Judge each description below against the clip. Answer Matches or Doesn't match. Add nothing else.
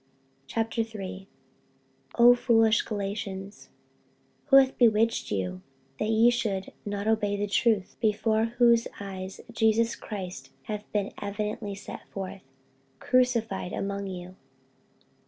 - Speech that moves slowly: Matches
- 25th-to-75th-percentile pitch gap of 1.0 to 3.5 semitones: Matches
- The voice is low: Doesn't match